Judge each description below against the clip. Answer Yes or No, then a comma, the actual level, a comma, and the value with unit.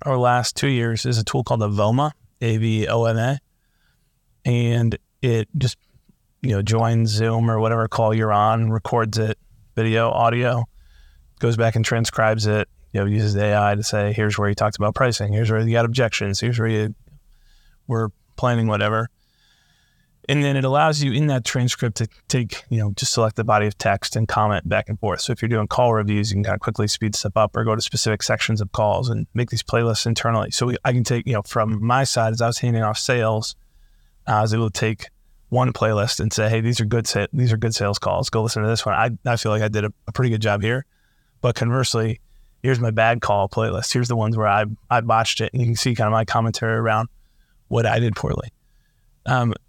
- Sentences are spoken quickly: Yes, fast, 230 wpm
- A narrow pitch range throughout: Yes, narrow, 2.2 semitones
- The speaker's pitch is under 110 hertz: No, low, 115 Hz